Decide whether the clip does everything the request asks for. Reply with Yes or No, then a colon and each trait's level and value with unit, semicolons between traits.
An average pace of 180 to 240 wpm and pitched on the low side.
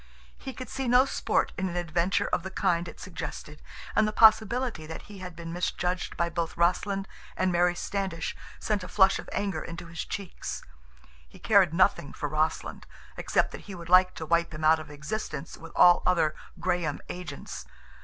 No: average, 185 wpm; medium, 175 Hz